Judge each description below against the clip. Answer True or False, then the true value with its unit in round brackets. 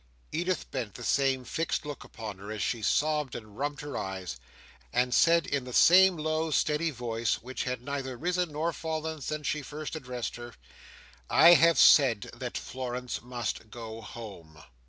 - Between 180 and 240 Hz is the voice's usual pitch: False (130 Hz)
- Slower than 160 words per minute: False (170 wpm)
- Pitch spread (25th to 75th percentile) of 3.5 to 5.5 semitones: True (4.9 semitones)